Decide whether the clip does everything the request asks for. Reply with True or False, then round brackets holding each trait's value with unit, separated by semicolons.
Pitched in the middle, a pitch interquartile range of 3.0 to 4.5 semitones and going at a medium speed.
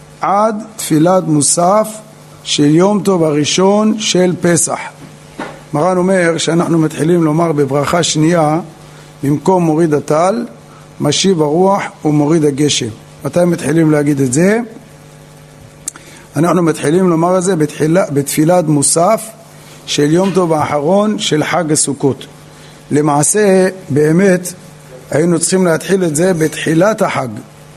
True (160 Hz; 3.8 semitones; 110 wpm)